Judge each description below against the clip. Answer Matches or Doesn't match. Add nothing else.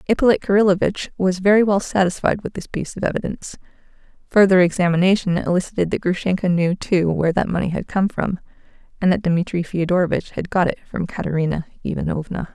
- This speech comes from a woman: Matches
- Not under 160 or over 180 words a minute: Matches